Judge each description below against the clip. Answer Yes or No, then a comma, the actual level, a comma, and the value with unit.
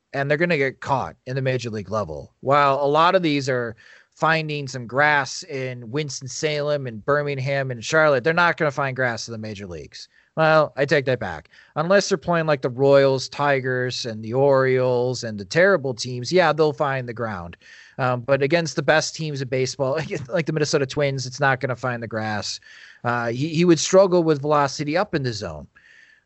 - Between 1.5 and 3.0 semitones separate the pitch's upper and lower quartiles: No, average, 3.5 semitones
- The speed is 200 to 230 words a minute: Yes, fast, 205 wpm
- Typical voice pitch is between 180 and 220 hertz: No, medium, 140 Hz